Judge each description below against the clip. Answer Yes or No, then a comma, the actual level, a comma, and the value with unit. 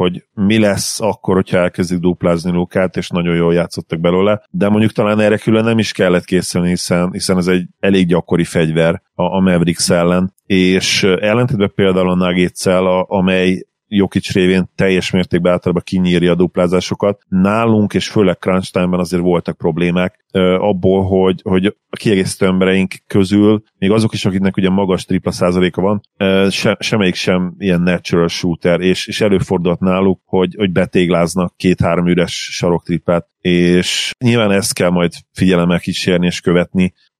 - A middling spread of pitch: No, narrow, 1.6 semitones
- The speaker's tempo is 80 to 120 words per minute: No, average, 150 wpm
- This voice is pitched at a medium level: No, very low, 95 Hz